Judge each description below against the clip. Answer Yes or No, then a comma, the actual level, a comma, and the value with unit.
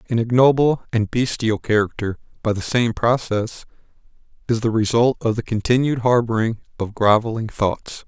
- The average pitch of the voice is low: Yes, low, 115 Hz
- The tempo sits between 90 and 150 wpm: Yes, average, 140 wpm